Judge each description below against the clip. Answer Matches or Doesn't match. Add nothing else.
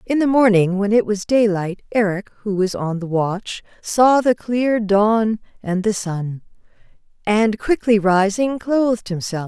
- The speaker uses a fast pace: Doesn't match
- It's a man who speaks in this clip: Doesn't match